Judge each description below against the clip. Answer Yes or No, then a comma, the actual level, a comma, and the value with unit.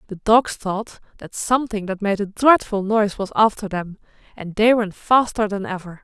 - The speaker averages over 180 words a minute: Yes, average, 190 wpm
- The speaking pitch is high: Yes, high, 205 Hz